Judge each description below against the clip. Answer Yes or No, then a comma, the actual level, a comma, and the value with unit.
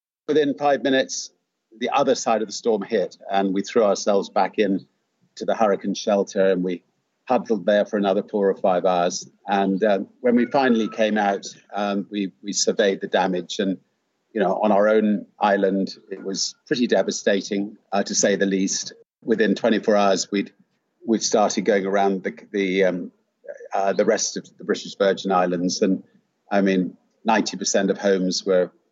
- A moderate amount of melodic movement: No, narrow, 1.4 semitones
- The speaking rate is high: No, average, 180 wpm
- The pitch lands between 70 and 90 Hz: No, low, 100 Hz